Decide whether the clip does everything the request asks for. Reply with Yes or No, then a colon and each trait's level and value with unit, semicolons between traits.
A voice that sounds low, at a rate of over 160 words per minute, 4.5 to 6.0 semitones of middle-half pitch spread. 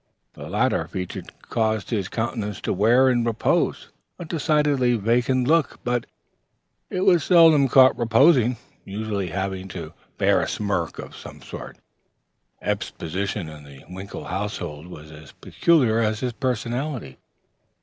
No: low, 115 Hz; average, 140 wpm; average, 5.2 semitones